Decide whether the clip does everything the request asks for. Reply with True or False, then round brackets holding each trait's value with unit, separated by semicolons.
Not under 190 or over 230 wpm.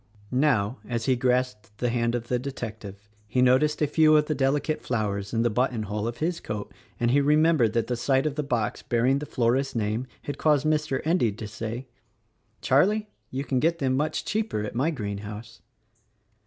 True (195 wpm)